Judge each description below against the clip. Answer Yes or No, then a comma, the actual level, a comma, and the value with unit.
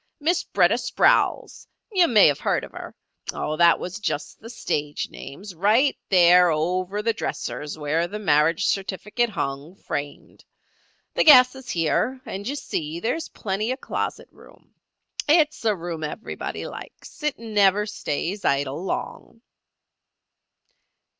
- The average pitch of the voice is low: No, high, 195 Hz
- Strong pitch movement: Yes, wide, 6.1 semitones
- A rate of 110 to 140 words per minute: Yes, slow, 135 wpm